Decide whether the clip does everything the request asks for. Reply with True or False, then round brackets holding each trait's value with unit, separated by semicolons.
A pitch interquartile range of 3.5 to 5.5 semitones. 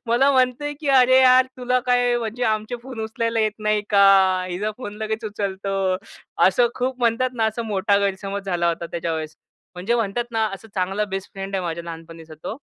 True (4.2 semitones)